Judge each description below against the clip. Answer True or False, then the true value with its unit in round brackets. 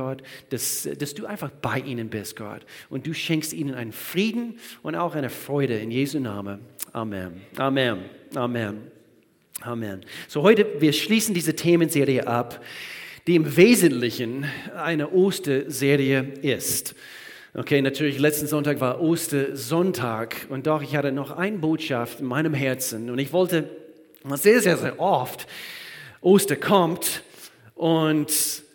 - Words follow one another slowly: False (135 wpm)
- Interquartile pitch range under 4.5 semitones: True (4.1 semitones)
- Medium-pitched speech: True (145 Hz)